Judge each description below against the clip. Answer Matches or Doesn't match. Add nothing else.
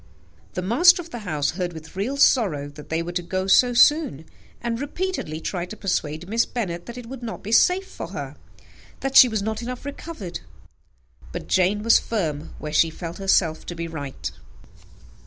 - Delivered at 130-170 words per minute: Doesn't match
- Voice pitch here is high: Matches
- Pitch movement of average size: Doesn't match